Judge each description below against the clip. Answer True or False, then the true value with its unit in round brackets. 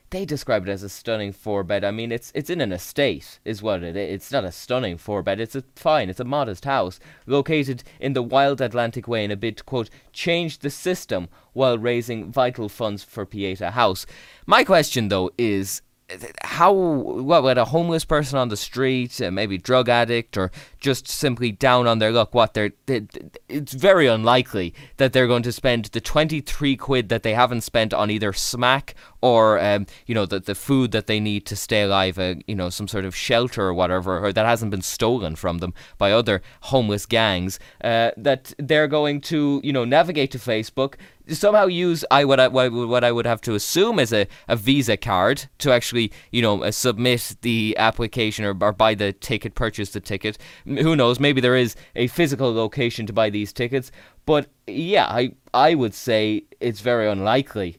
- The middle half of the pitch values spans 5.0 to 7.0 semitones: False (4.4 semitones)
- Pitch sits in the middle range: False (115 Hz)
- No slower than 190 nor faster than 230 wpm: True (200 wpm)